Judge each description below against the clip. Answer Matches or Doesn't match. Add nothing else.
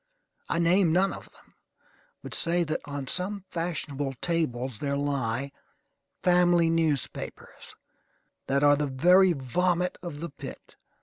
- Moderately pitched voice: Matches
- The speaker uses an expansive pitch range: Doesn't match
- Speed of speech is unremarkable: Doesn't match